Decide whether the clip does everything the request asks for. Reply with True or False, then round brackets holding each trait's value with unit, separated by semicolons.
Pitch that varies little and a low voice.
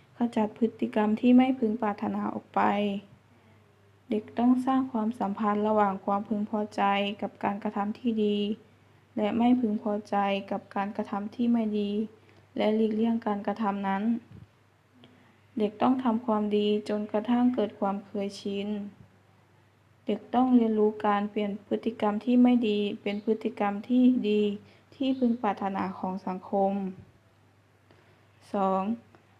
False (2.3 semitones; 205 Hz)